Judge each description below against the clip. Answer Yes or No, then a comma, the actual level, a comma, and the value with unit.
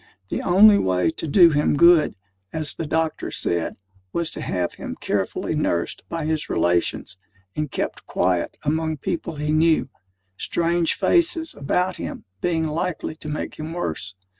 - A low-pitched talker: No, medium, 155 Hz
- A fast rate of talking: No, average, 155 wpm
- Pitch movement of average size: Yes, average, 3.2 semitones